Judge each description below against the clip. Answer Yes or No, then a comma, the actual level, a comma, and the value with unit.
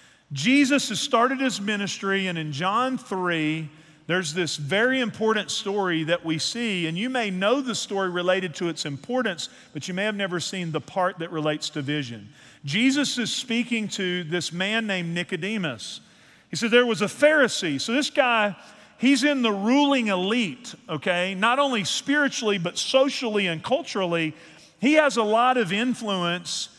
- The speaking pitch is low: No, high, 200 Hz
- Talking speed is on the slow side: No, average, 170 wpm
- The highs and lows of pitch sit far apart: Yes, wide, 5.8 semitones